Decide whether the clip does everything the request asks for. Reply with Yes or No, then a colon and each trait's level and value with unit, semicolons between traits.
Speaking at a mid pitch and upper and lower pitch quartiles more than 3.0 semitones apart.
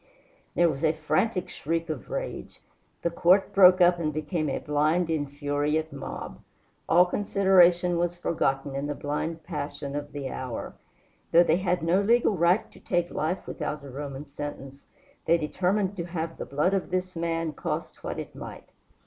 Yes: medium, 165 Hz; average, 3.4 semitones